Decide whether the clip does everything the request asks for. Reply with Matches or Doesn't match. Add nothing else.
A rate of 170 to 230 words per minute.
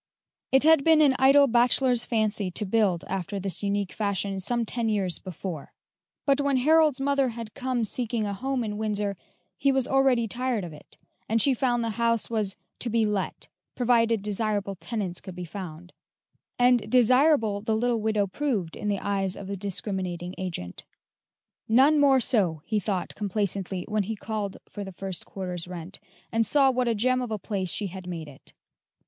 Matches